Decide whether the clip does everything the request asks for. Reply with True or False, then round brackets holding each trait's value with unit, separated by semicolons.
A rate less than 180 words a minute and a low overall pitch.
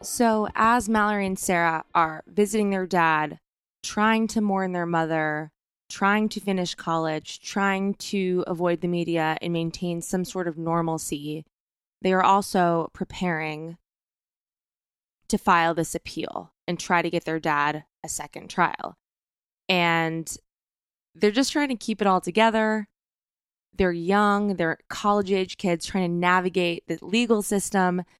False (145 wpm; 180 Hz)